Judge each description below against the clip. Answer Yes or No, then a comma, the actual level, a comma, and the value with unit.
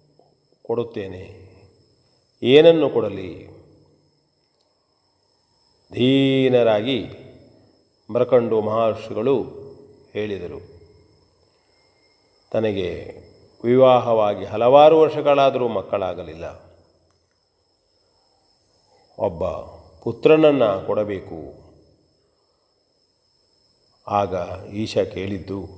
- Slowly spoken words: Yes, slow, 40 wpm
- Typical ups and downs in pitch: Yes, average, 4.8 semitones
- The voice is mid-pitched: No, low, 115 Hz